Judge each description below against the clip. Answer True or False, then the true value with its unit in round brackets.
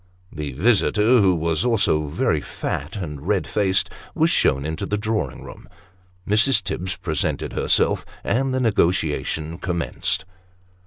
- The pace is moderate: False (125 wpm)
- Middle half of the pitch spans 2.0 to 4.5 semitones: False (5.3 semitones)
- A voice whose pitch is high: False (95 Hz)